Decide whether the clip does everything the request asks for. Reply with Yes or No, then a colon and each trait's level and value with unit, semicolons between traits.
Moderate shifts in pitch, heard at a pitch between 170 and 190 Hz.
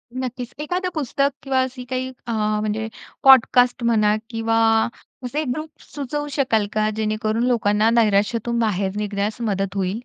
No: average, 3.4 semitones; high, 230 Hz